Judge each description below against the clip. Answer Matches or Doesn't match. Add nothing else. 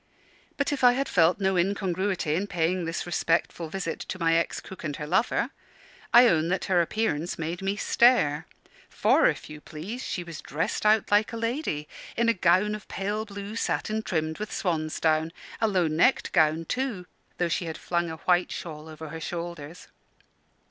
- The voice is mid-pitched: Matches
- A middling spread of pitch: Matches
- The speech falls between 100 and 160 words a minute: Doesn't match